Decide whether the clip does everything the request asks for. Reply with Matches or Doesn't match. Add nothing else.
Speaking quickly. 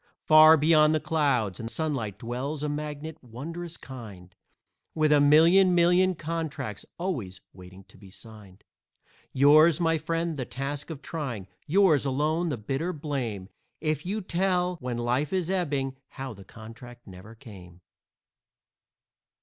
Doesn't match